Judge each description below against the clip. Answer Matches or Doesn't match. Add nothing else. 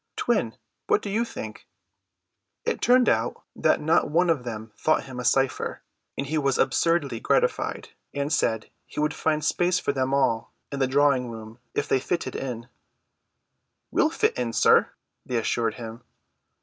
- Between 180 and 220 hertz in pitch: Doesn't match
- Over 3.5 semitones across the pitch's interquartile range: Matches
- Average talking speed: Matches